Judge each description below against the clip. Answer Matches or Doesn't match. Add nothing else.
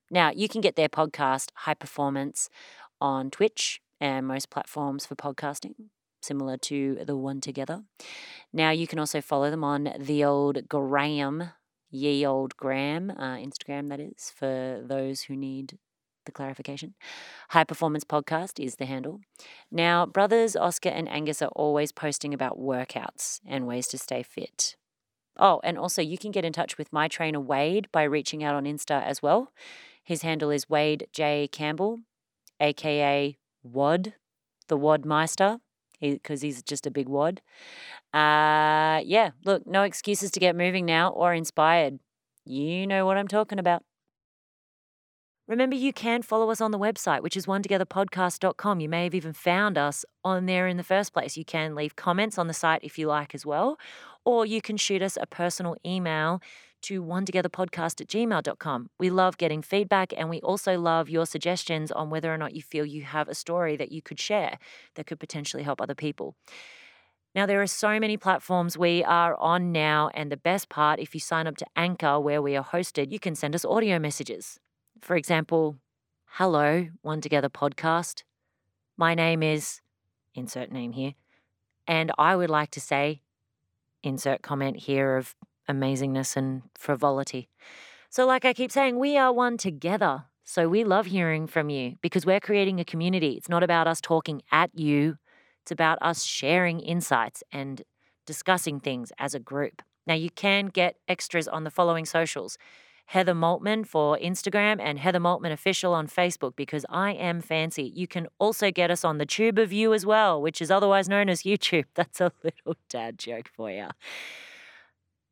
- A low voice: Doesn't match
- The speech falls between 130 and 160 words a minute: Doesn't match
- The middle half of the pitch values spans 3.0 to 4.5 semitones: Matches